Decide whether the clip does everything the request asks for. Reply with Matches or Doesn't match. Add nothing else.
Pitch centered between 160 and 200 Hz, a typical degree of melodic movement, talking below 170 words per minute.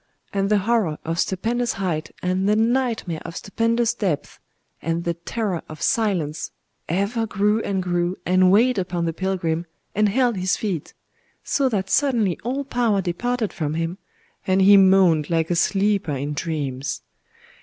Matches